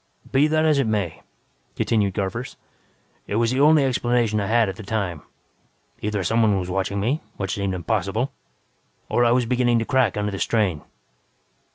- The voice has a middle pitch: No, low, 110 Hz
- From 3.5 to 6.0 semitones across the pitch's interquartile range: Yes, average, 3.8 semitones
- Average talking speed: Yes, average, 175 wpm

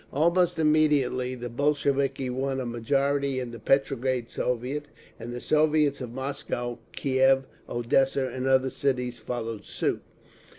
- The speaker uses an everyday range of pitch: No, narrow, 2.3 semitones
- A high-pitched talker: No, low, 130 Hz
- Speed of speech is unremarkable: No, slow, 130 wpm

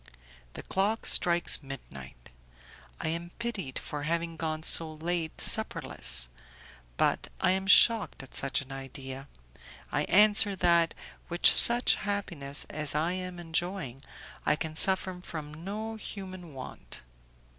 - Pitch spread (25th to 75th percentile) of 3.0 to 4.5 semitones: No, average, 4.9 semitones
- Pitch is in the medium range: Yes, medium, 165 Hz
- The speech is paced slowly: Yes, slow, 130 wpm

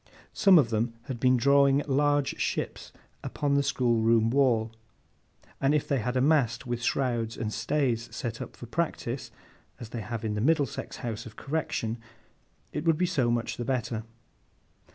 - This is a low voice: Yes, low, 125 Hz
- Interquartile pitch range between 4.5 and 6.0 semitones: No, average, 3.5 semitones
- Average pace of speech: Yes, average, 170 wpm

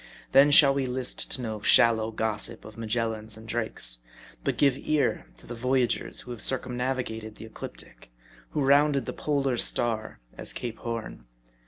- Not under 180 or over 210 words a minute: No, average, 165 wpm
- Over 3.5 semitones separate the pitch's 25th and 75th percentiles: No, average, 3.1 semitones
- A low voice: Yes, low, 120 Hz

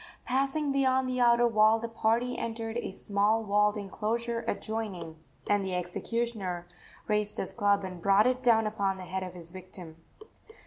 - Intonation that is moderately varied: Yes, average, 3.6 semitones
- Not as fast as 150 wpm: No, average, 165 wpm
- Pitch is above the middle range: Yes, high, 215 Hz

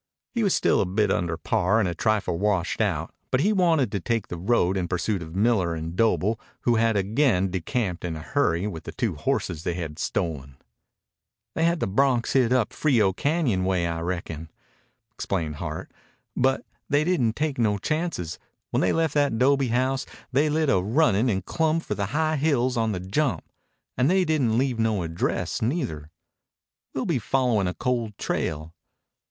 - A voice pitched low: Yes, low, 110 Hz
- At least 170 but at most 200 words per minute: Yes, average, 180 wpm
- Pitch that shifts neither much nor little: No, wide, 7.1 semitones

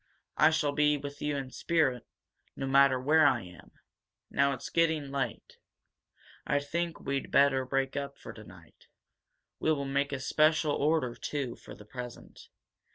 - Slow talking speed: No, average, 160 wpm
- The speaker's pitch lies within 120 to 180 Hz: Yes, medium, 140 Hz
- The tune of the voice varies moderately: No, narrow, 2.0 semitones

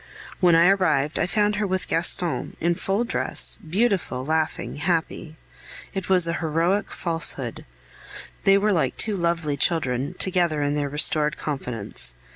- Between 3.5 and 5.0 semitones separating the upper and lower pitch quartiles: Yes, average, 3.9 semitones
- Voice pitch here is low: No, medium, 170 Hz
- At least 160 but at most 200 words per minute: No, average, 145 wpm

